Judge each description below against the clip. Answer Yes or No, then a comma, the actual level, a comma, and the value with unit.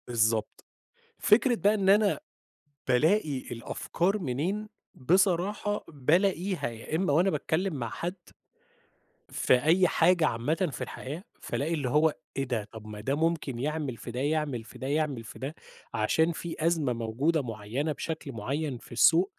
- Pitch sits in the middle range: Yes, medium, 150 Hz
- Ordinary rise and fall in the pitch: No, wide, 5.9 semitones